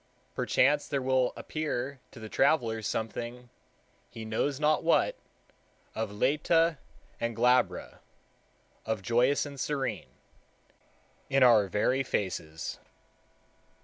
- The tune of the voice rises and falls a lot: No, average, 4.0 semitones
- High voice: No, low, 125 Hz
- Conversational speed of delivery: No, slow, 105 wpm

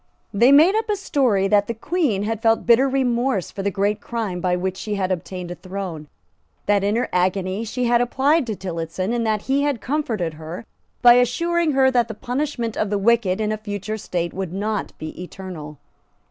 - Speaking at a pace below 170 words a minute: No, average, 200 wpm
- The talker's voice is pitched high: Yes, high, 215 Hz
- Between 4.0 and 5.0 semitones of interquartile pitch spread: Yes, average, 4.6 semitones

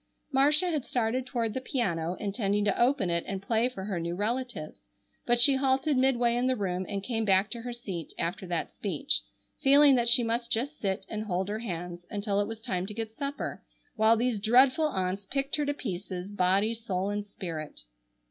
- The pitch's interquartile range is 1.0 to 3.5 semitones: No, average, 4.8 semitones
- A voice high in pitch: Yes, high, 220 Hz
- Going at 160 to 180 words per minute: No, average, 200 wpm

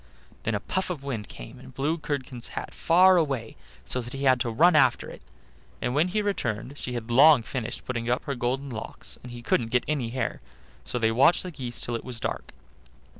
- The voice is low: Yes, low, 125 Hz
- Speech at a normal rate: No, fast, 220 wpm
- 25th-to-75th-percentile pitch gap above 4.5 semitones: No, average, 4.0 semitones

